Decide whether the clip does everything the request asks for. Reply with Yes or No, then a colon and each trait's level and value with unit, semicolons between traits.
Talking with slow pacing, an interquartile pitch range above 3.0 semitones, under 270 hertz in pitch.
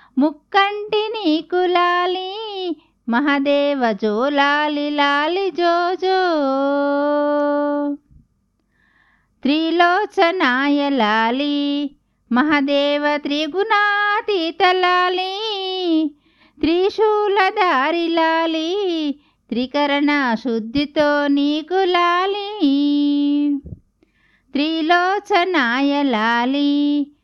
No: slow, 35 wpm; average, 4.1 semitones; very high, 300 Hz